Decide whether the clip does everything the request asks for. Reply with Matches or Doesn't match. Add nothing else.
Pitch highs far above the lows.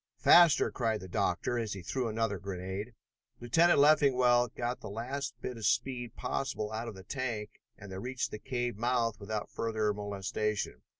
Doesn't match